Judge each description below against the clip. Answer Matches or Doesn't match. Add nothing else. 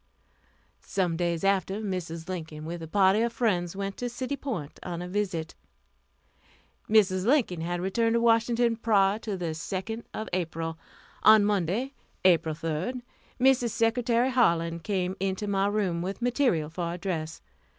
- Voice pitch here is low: Doesn't match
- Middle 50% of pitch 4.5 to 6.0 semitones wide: Matches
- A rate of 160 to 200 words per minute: Doesn't match